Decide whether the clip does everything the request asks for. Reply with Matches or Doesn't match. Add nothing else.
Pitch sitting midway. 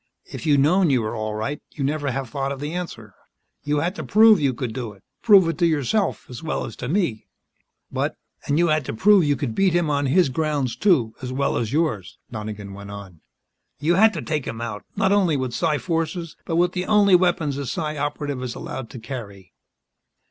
Matches